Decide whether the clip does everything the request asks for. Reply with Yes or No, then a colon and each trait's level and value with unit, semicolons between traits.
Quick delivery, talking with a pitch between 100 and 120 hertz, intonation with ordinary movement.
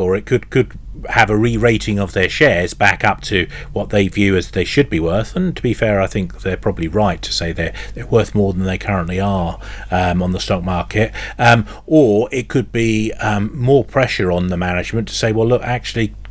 Yes: fast, 230 wpm; low, 105 Hz; average, 3.9 semitones